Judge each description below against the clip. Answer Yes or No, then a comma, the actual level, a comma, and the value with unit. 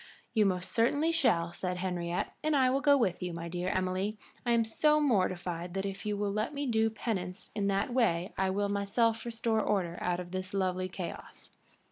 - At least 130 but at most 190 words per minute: No, average, 200 wpm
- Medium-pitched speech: No, high, 200 Hz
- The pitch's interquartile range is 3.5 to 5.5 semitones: Yes, average, 4.1 semitones